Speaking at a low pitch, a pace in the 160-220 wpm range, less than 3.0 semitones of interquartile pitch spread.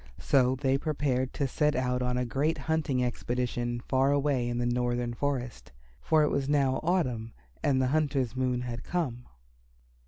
Yes: low, 130 Hz; average, 165 wpm; narrow, 2.6 semitones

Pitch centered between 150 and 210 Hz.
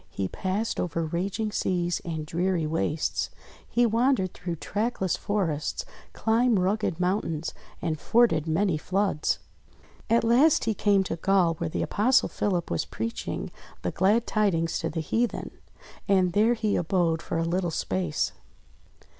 Yes: medium, 185 Hz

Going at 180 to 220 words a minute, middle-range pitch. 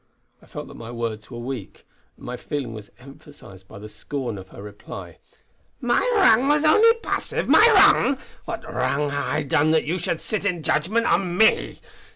Yes: average, 190 wpm; medium, 145 Hz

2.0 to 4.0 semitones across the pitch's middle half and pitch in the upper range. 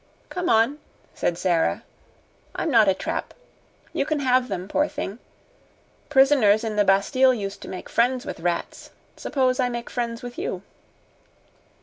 No: average, 4.8 semitones; high, 235 Hz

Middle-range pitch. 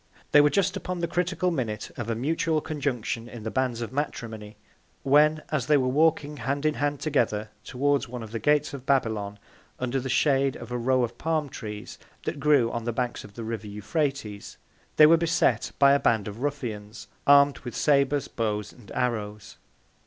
No: low, 130 Hz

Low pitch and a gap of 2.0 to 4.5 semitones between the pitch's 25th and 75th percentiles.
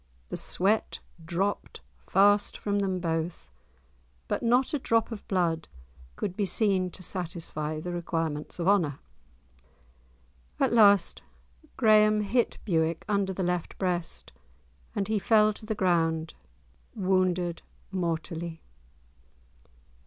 No: medium, 185 Hz; average, 3.6 semitones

